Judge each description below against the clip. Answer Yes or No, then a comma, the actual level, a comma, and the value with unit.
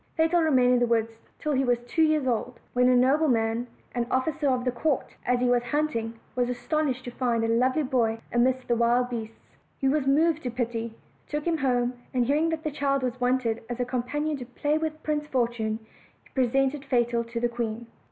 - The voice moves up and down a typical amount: Yes, average, 3.2 semitones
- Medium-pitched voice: No, very high, 250 Hz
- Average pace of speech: No, fast, 215 wpm